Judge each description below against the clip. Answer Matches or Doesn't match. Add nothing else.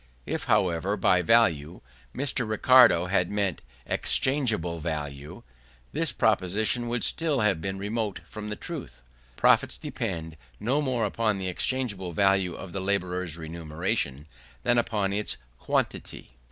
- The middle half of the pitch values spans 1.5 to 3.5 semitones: Doesn't match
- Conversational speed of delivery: Doesn't match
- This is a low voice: Matches